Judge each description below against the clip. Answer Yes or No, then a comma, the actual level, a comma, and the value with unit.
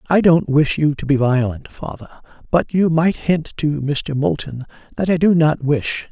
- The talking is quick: No, average, 195 wpm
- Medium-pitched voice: Yes, medium, 150 Hz